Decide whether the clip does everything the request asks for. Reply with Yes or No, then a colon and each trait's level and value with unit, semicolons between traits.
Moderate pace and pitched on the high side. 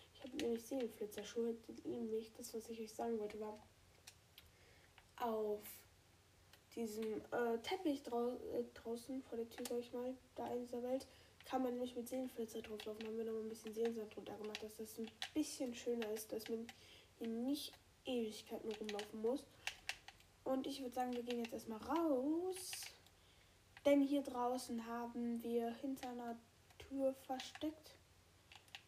Yes: average, 160 wpm; high, 235 Hz